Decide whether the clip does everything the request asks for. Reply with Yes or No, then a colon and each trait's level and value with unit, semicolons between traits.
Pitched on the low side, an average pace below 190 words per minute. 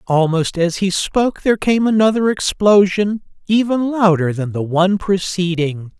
No: high, 190 Hz; average, 140 wpm